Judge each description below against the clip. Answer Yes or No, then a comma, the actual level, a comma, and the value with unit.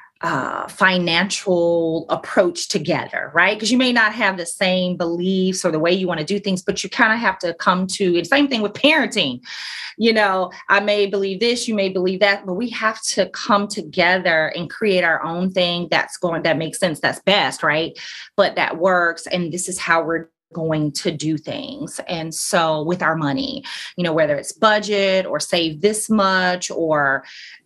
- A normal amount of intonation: Yes, average, 3.4 semitones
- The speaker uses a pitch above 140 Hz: Yes, medium, 185 Hz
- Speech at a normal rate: Yes, average, 195 wpm